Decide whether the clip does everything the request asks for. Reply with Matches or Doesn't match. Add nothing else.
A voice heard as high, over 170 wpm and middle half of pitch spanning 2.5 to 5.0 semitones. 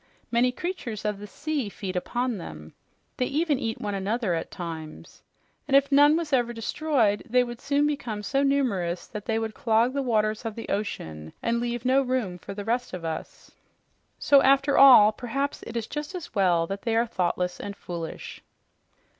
Doesn't match